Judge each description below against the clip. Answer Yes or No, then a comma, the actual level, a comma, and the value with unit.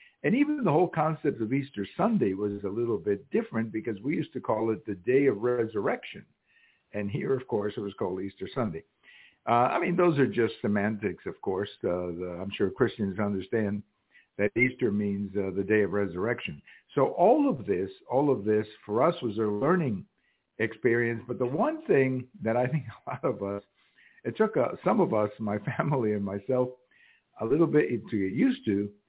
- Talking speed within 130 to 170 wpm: No, average, 200 wpm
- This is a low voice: Yes, low, 115 Hz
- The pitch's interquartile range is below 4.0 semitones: No, average, 5.0 semitones